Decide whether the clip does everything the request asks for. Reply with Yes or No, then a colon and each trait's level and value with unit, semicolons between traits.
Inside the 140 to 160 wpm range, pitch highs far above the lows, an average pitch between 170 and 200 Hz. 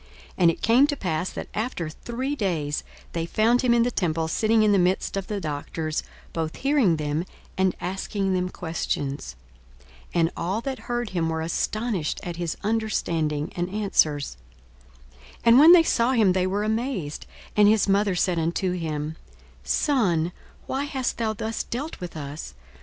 No: average, 175 wpm; wide, 5.7 semitones; medium, 185 Hz